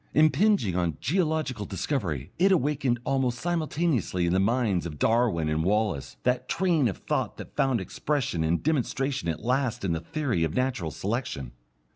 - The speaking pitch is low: Yes, low, 120 Hz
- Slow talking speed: No, average, 160 wpm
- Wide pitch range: Yes, wide, 8.5 semitones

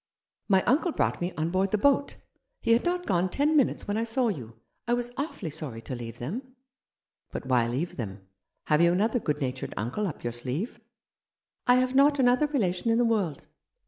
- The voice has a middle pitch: No, high, 195 Hz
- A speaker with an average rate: No, fast, 210 wpm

